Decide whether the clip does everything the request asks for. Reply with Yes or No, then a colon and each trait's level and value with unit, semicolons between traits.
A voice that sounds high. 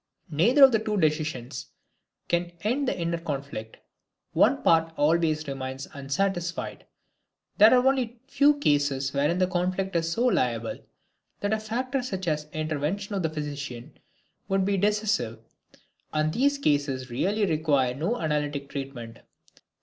No: medium, 165 Hz